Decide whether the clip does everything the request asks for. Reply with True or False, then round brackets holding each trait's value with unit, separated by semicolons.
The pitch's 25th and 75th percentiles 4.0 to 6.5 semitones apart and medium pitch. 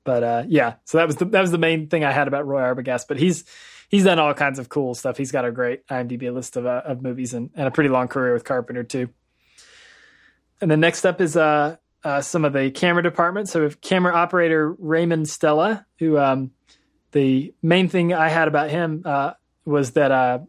True (4.5 semitones; 145 Hz)